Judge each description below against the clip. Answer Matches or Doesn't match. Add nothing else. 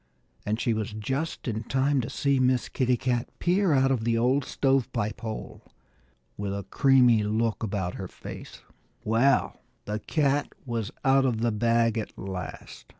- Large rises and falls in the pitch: Doesn't match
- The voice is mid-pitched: Doesn't match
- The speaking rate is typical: Matches